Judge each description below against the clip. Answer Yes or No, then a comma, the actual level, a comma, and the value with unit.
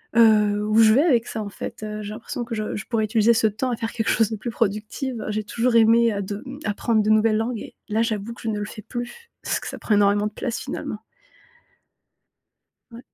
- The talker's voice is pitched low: No, high, 220 Hz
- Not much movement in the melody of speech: Yes, narrow, 1.7 semitones